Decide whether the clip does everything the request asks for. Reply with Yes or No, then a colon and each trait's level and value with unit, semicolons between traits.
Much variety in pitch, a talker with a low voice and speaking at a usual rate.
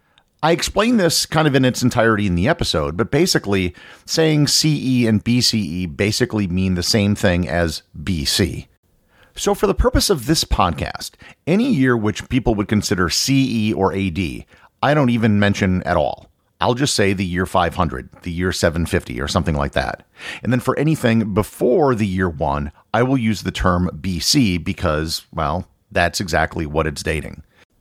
Yes: wide, 5.7 semitones; low, 100 Hz; average, 175 wpm